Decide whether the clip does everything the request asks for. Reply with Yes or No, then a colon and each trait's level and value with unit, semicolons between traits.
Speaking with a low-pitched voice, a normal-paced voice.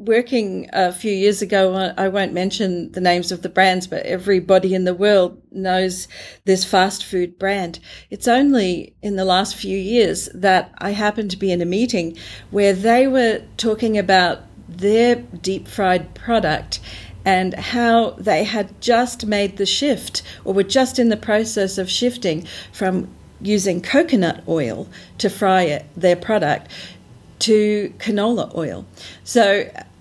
No: high, 195 Hz; average, 150 wpm